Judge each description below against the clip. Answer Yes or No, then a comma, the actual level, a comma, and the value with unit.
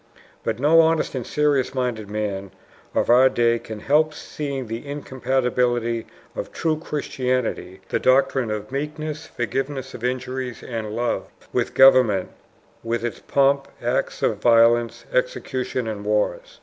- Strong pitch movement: No, average, 3.2 semitones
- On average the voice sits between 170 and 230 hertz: No, low, 125 Hz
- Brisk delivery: No, slow, 135 wpm